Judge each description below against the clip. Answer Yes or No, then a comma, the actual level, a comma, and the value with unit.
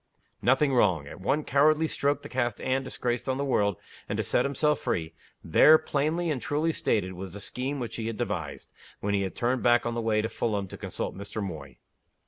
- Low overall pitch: Yes, low, 120 Hz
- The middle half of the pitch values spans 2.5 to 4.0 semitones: No, wide, 5.6 semitones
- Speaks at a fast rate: Yes, fast, 215 wpm